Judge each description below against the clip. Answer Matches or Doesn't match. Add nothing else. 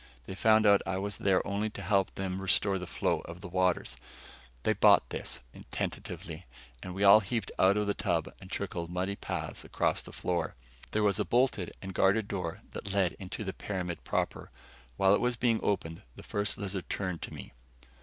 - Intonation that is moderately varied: Doesn't match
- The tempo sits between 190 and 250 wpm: Matches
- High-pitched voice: Doesn't match